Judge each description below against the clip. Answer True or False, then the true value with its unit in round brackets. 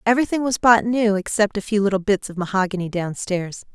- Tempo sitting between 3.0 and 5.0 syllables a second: False (5.9 syllables/s)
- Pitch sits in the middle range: False (205 Hz)